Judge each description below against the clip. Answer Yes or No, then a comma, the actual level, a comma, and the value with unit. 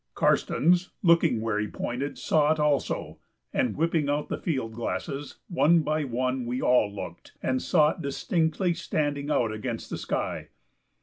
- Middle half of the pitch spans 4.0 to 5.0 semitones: Yes, average, 4.4 semitones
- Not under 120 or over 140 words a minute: No, average, 160 wpm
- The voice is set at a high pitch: No, medium, 145 Hz